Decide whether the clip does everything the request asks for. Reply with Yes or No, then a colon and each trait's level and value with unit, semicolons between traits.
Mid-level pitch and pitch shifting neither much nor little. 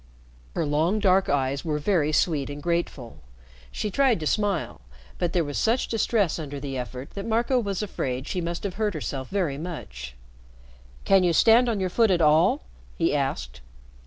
No: medium, 170 Hz; wide, 5.9 semitones